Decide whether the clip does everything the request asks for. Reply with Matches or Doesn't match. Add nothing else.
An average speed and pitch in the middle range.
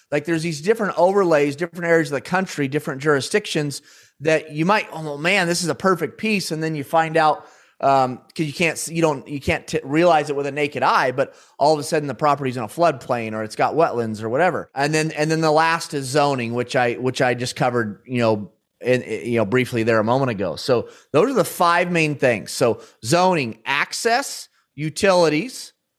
Doesn't match